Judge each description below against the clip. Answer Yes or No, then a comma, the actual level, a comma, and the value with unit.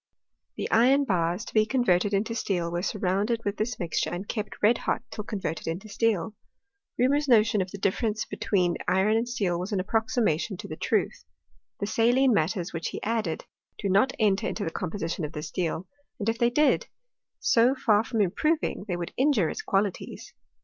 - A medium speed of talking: Yes, average, 190 wpm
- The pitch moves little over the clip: No, average, 3.9 semitones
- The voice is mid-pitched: No, high, 210 Hz